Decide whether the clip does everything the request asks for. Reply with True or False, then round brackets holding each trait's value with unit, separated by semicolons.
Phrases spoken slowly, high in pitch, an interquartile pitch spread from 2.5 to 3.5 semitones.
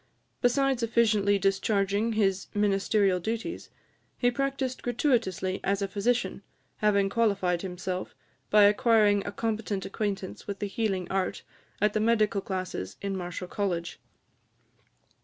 True (120 wpm; 205 Hz; 2.8 semitones)